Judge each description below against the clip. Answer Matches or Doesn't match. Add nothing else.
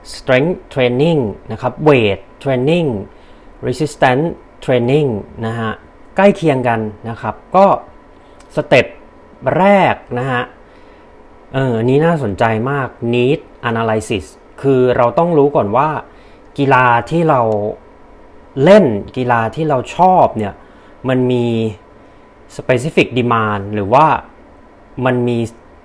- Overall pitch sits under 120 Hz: Doesn't match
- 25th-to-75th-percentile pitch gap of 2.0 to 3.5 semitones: Doesn't match